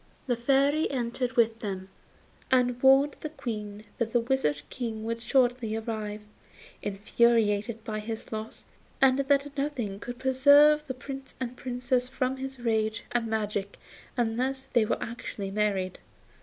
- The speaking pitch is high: Yes, high, 240 Hz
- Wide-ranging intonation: No, average, 3.4 semitones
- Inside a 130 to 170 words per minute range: Yes, average, 140 wpm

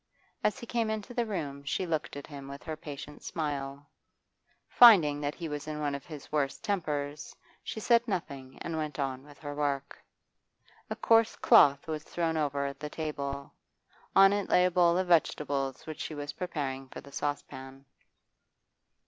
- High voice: No, medium, 150 Hz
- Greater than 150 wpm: Yes, average, 175 wpm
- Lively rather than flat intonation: No, average, 3.7 semitones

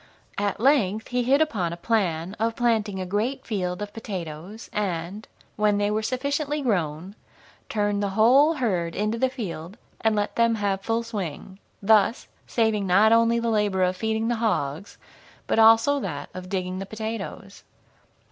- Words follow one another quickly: No, average, 165 wpm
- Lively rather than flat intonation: No, average, 3.4 semitones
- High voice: Yes, high, 210 Hz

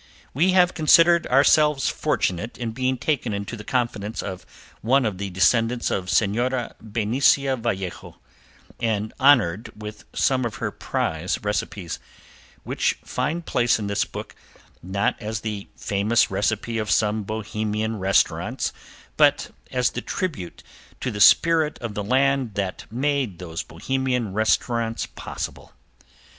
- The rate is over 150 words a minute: No, slow, 135 wpm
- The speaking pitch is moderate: No, low, 115 Hz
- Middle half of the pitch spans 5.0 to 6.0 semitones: No, average, 4.3 semitones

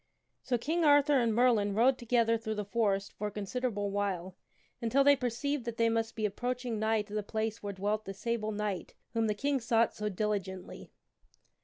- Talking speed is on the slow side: No, average, 195 wpm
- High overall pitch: Yes, high, 220 Hz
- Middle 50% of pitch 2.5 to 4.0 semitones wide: Yes, average, 2.9 semitones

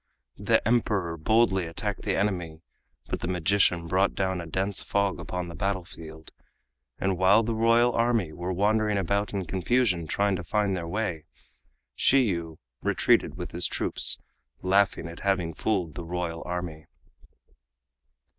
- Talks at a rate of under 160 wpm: Yes, average, 145 wpm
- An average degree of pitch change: Yes, average, 3.3 semitones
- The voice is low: Yes, very low, 95 Hz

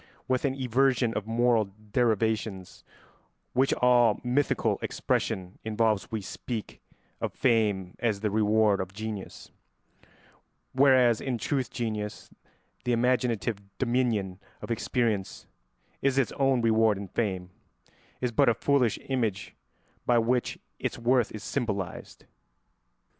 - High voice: No, low, 115 Hz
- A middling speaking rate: No, slow, 120 wpm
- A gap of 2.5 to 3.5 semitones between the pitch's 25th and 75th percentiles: Yes, average, 3.0 semitones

